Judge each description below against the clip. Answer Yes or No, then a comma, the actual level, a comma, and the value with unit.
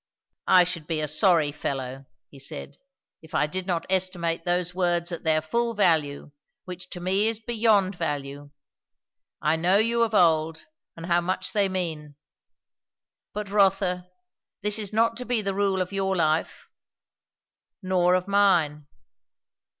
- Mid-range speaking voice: Yes, medium, 180 Hz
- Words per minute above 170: No, average, 150 wpm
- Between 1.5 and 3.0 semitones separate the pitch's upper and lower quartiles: No, average, 3.8 semitones